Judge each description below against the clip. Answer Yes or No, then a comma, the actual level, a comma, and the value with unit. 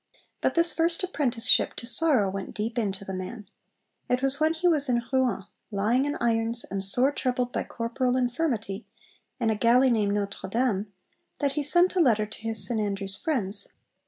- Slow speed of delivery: No, average, 185 wpm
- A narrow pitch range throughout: No, average, 4.6 semitones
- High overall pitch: Yes, high, 235 Hz